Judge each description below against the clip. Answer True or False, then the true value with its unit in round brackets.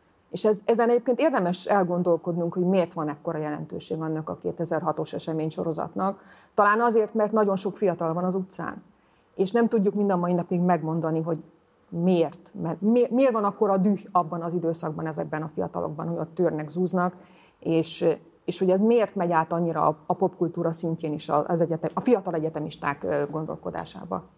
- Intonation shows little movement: False (3.2 semitones)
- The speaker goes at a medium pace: False (170 wpm)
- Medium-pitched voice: True (175 Hz)